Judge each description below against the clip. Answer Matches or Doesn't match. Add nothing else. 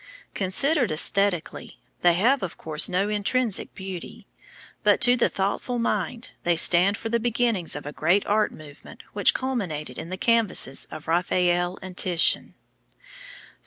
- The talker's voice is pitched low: Doesn't match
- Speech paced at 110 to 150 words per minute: Matches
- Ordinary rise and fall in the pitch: Matches